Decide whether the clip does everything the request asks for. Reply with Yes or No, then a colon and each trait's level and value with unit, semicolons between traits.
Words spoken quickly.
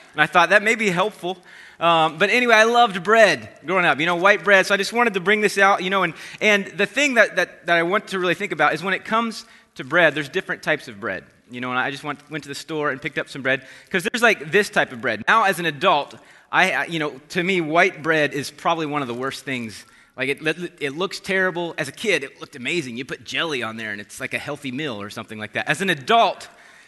Yes: fast, 270 wpm